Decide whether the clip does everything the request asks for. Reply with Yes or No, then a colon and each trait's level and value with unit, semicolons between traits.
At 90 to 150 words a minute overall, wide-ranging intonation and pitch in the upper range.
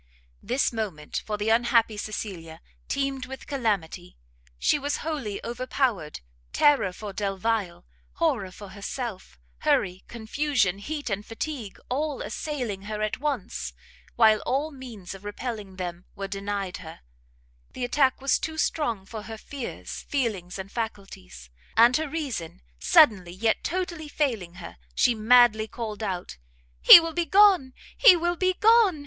Yes: average, 140 wpm; wide, 6.1 semitones; high, 225 Hz